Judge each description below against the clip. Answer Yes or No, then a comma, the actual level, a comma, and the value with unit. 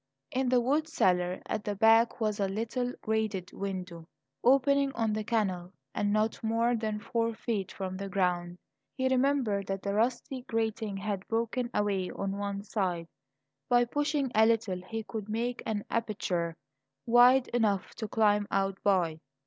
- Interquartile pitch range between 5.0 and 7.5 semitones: No, average, 3.3 semitones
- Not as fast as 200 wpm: Yes, average, 160 wpm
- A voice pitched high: Yes, high, 215 Hz